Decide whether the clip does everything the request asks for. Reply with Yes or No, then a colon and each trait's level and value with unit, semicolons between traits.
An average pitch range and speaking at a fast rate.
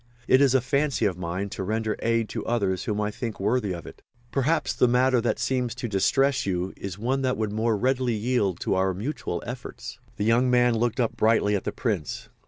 Yes: average, 3.8 semitones; fast, 215 wpm